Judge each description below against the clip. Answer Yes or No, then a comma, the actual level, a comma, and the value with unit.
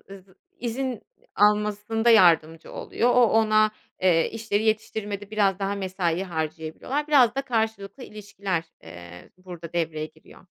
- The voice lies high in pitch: Yes, high, 200 Hz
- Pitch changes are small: No, average, 4.5 semitones